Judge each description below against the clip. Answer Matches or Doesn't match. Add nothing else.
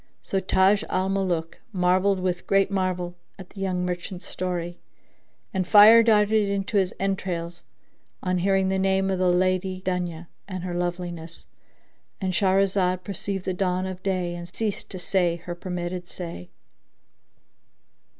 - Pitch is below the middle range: Doesn't match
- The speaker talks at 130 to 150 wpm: Matches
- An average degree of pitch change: Doesn't match